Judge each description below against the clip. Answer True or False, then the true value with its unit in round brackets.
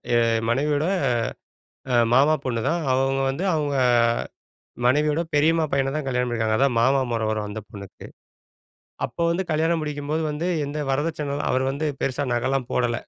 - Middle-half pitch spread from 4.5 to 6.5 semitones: False (3.8 semitones)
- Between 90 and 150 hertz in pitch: True (140 Hz)